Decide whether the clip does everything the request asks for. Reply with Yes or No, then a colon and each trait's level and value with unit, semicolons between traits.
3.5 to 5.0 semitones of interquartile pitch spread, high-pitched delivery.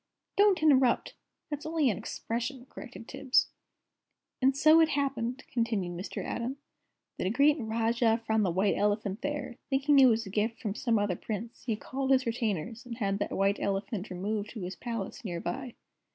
Yes: average, 4.4 semitones; high, 230 Hz